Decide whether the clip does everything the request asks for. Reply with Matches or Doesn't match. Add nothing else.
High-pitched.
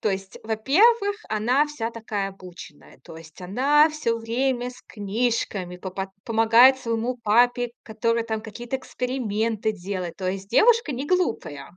Matches